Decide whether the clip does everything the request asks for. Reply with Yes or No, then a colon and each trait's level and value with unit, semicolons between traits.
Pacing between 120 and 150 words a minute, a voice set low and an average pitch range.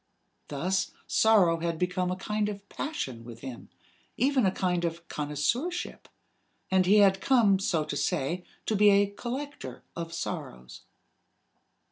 No: average, 140 wpm; medium, 185 Hz; average, 4.2 semitones